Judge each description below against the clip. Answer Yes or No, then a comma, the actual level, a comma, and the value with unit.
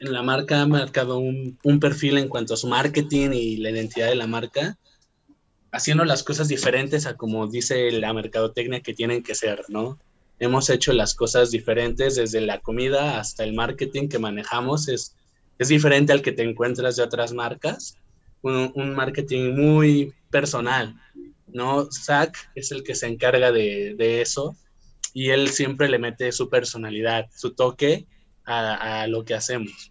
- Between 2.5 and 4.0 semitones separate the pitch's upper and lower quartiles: Yes, average, 3.4 semitones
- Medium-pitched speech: No, low, 125 Hz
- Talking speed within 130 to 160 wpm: No, average, 170 wpm